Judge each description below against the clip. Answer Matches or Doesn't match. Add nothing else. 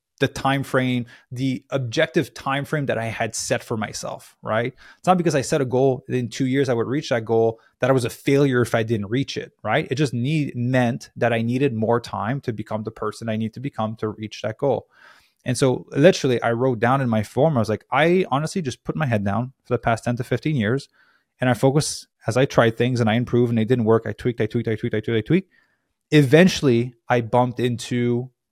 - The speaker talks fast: Matches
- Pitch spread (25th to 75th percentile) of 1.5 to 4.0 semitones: Matches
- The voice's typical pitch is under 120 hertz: Doesn't match